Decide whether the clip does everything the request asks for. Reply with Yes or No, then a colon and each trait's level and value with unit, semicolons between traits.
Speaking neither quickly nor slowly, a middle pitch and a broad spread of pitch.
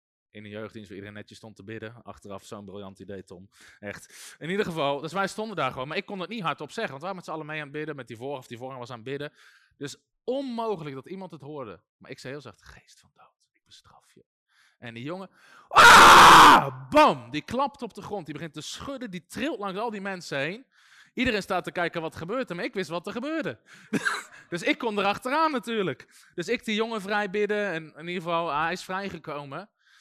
No: fast, 240 wpm; medium, 165 Hz; wide, 7.9 semitones